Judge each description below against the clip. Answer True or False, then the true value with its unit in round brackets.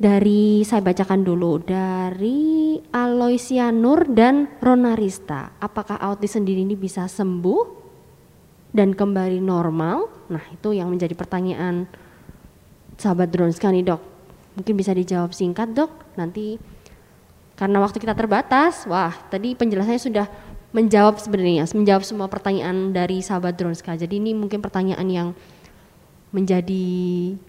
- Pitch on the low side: False (195 Hz)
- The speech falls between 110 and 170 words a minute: True (120 wpm)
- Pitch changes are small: False (3.1 semitones)